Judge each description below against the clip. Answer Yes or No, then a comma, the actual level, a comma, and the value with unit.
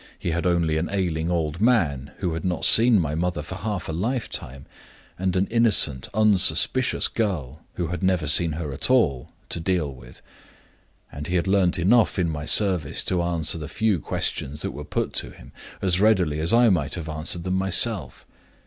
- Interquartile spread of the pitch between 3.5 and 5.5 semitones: Yes, average, 3.9 semitones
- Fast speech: No, average, 190 wpm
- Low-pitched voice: Yes, very low, 85 Hz